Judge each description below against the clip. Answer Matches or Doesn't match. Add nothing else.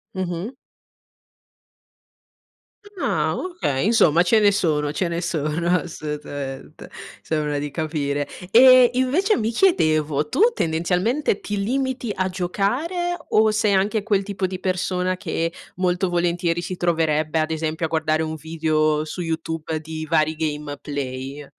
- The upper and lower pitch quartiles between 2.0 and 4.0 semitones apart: Doesn't match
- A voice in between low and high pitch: Matches